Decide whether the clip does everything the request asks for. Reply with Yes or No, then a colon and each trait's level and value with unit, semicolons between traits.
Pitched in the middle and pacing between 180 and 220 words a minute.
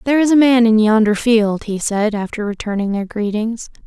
No: high, 220 Hz; average, 200 wpm